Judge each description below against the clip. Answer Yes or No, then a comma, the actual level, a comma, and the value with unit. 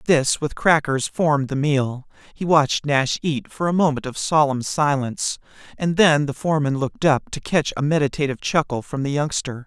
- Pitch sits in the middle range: Yes, medium, 145 Hz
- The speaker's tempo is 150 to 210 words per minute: Yes, average, 185 wpm